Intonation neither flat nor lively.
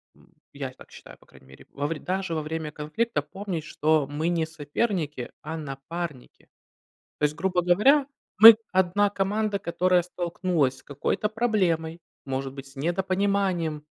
Yes: average, 4.3 semitones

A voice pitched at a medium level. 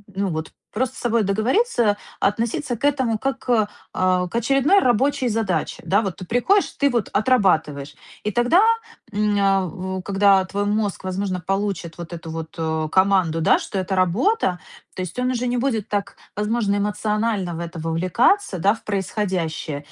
No: high, 200 Hz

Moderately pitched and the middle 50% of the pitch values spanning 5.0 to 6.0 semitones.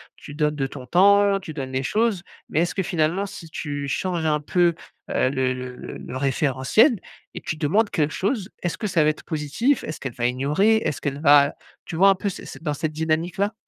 Yes: medium, 155 Hz; average, 5.3 semitones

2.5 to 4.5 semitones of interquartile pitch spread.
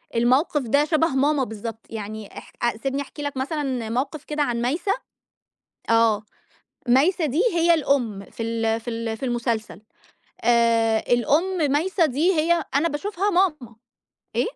No: average, 5.2 semitones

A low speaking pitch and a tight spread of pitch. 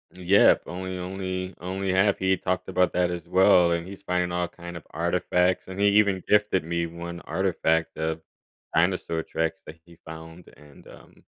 Yes: very low, 90 Hz; narrow, 1.9 semitones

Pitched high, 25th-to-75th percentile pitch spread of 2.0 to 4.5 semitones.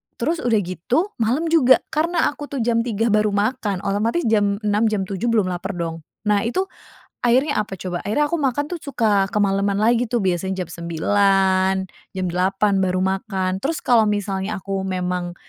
Yes: high, 205 Hz; average, 3.9 semitones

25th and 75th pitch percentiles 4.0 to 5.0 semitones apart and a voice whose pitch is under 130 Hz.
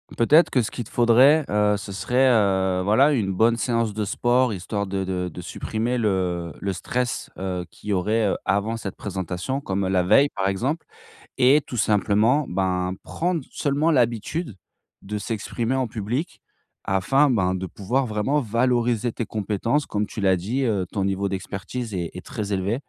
Yes: average, 4.4 semitones; low, 105 Hz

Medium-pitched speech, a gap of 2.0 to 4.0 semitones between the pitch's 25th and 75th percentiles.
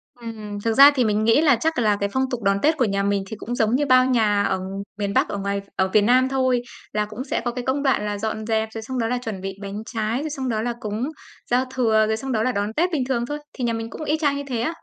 No: high, 230 Hz; average, 3.6 semitones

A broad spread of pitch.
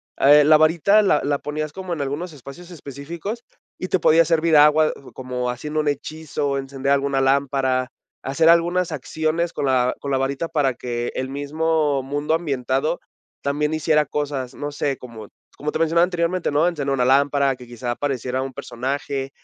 No: average, 2.8 semitones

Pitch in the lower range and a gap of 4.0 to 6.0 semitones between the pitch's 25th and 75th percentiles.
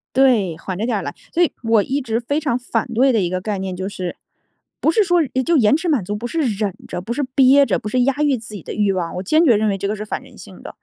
No: high, 225 Hz; wide, 5.6 semitones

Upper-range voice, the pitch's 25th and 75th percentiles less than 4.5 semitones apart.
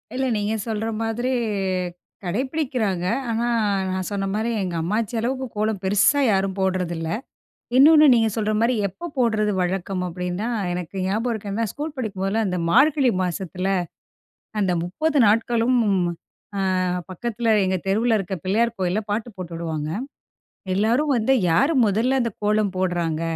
Yes: high, 210 Hz; average, 4.1 semitones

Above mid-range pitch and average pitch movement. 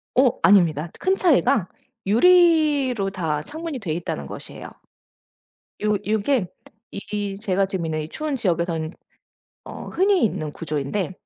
No: high, 200 Hz; wide, 8.6 semitones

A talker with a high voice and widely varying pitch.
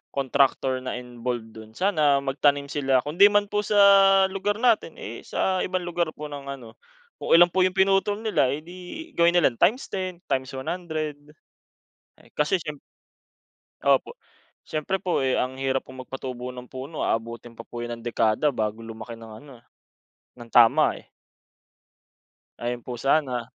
No: medium, 140 Hz; wide, 6.2 semitones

